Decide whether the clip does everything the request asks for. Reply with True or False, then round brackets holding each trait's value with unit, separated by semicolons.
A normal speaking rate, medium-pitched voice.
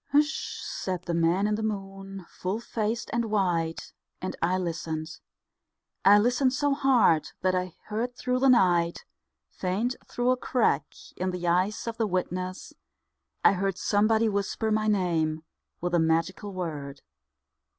False (150 wpm; 195 Hz)